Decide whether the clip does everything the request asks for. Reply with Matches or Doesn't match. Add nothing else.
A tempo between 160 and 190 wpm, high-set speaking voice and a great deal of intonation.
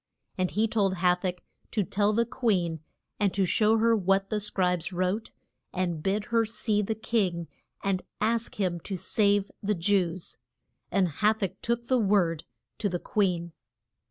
Doesn't match